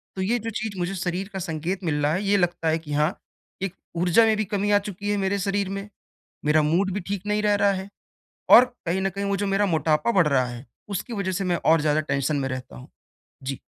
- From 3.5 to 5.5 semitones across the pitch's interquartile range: Yes, average, 4.4 semitones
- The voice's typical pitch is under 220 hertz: Yes, high, 190 Hz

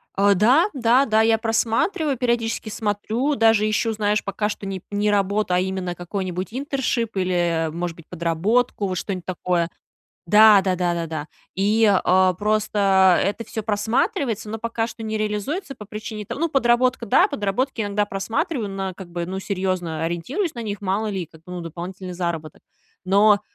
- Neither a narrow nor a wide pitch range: Yes, average, 3.5 semitones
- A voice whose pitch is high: Yes, high, 205 Hz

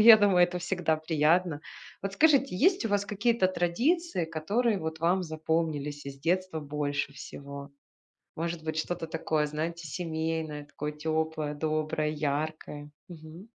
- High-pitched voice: No, medium, 160 Hz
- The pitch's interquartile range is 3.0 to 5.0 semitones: Yes, average, 3.3 semitones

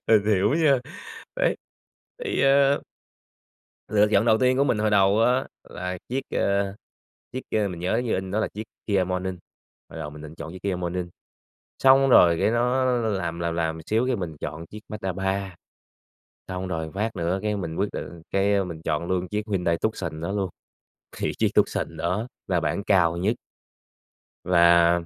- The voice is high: No, very low, 95 Hz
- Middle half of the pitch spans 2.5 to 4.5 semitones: Yes, average, 4.1 semitones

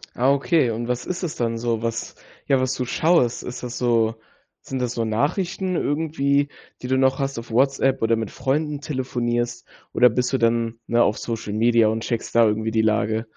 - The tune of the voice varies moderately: Yes, average, 3.0 semitones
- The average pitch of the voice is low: Yes, low, 120 Hz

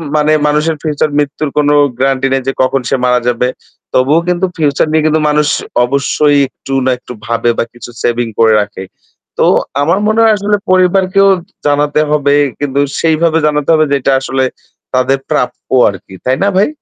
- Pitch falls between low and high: Yes, medium, 145 Hz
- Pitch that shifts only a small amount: No, average, 3.2 semitones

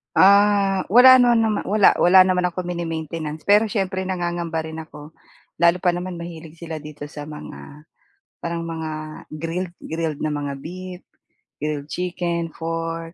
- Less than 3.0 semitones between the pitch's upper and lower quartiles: Yes, narrow, 2.4 semitones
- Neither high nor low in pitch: Yes, medium, 170 Hz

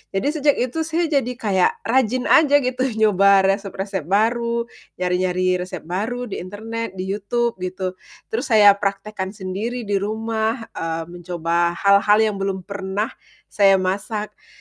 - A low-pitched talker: No, high, 200 Hz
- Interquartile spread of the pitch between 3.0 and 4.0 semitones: Yes, average, 3.5 semitones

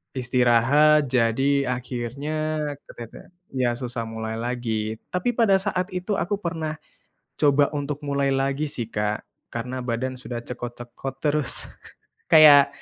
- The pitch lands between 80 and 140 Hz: Yes, low, 135 Hz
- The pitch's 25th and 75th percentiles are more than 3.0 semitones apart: Yes, average, 4.1 semitones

